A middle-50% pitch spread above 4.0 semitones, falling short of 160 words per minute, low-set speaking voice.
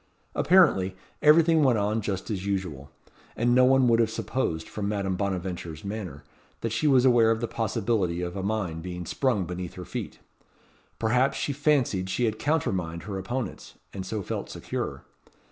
No: average, 4.9 semitones; average, 170 wpm; low, 105 Hz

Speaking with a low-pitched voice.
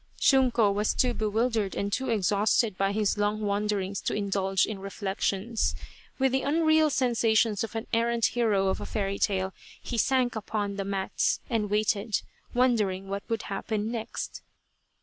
No: high, 215 Hz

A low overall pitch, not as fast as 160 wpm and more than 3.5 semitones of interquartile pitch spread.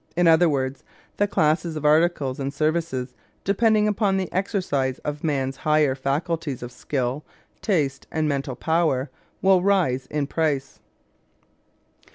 No: medium, 155 Hz; slow, 135 wpm; average, 4.2 semitones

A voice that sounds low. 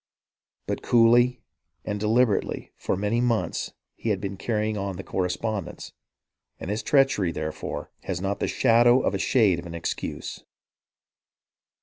Yes: low, 105 Hz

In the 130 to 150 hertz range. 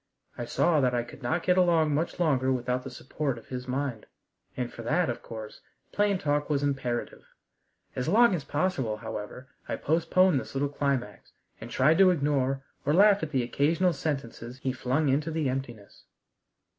Yes: medium, 140 Hz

